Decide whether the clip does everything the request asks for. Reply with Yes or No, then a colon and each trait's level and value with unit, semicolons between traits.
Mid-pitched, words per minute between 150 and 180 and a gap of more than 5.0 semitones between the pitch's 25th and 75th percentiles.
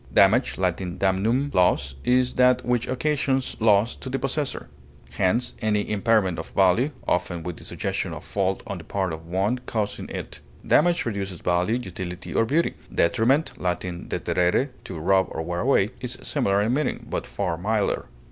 No: low, 105 Hz; average, 170 wpm; wide, 5.6 semitones